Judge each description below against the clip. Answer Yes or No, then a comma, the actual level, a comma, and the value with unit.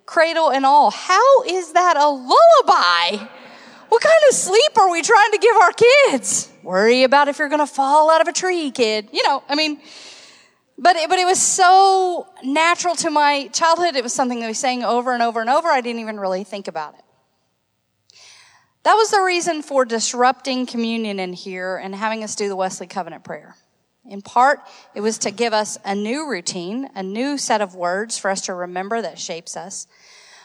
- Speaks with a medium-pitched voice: No, very high, 260 Hz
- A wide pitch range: Yes, wide, 7.7 semitones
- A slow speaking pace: No, average, 200 wpm